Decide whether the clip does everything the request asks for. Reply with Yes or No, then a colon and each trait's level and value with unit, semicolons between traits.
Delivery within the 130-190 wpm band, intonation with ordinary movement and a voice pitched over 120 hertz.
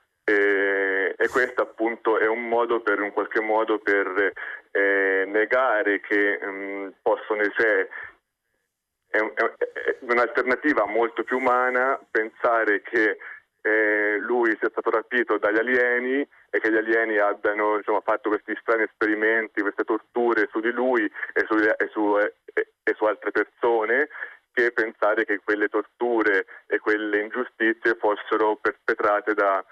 No: average, 135 wpm; average, 3.0 semitones; low, 110 Hz